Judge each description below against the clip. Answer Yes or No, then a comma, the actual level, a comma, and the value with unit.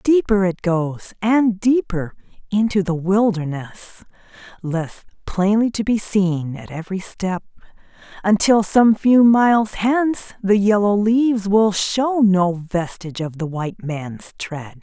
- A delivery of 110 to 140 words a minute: Yes, slow, 135 wpm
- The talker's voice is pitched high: Yes, high, 200 Hz